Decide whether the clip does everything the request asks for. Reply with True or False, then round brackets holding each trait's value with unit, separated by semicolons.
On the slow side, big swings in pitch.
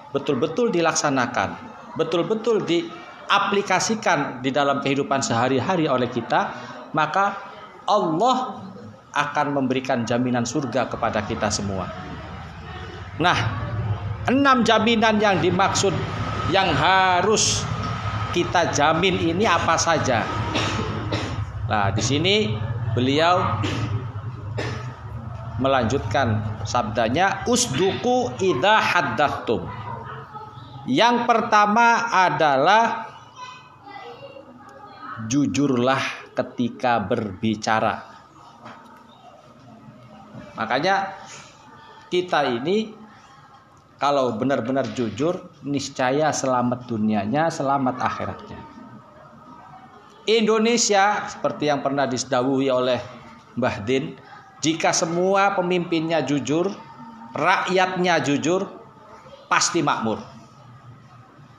True (70 wpm; 8.5 semitones)